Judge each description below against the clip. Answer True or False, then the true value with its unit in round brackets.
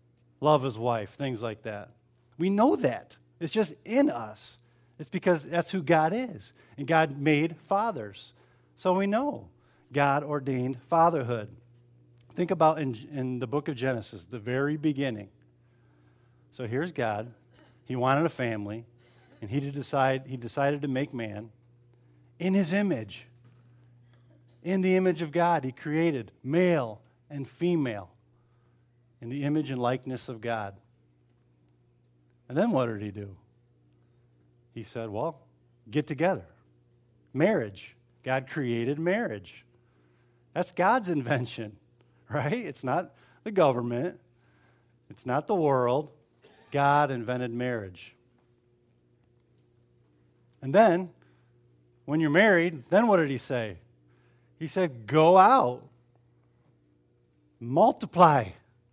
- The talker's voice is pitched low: True (120 Hz)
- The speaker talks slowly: True (125 wpm)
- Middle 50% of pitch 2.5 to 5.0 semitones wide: False (5.5 semitones)